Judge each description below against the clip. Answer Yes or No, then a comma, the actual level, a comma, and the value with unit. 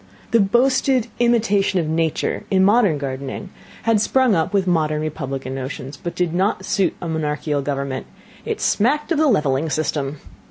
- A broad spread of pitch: Yes, wide, 6.6 semitones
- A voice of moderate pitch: Yes, medium, 165 Hz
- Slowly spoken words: No, average, 160 wpm